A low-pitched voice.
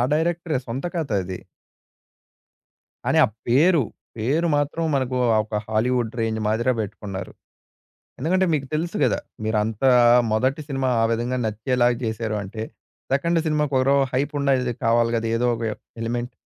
Yes: low, 125 Hz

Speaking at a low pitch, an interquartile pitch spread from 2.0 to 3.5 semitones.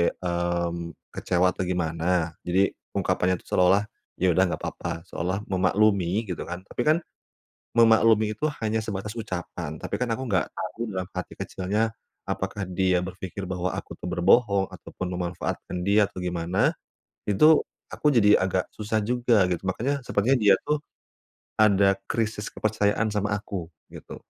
Yes: very low, 95 Hz; average, 3.2 semitones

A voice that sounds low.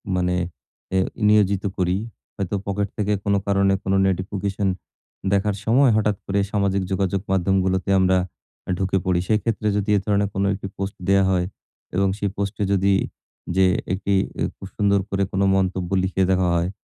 Yes: very low, 95 Hz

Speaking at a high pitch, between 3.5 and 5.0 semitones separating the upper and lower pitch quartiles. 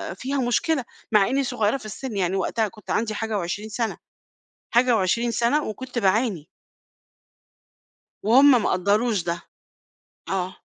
Yes: high, 220 Hz; average, 3.9 semitones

